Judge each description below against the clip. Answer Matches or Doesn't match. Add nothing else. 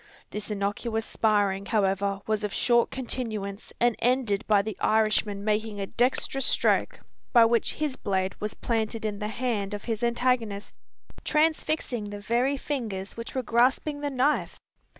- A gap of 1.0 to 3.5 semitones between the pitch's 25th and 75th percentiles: Matches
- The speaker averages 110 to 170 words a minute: Matches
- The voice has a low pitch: Doesn't match